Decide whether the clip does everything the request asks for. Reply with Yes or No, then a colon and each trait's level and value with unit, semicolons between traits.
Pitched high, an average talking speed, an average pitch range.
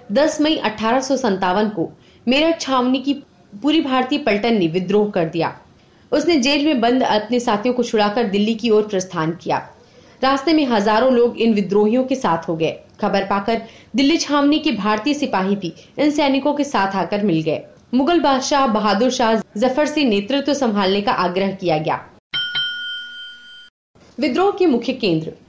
No: high, 240 Hz; average, 160 wpm; wide, 5.9 semitones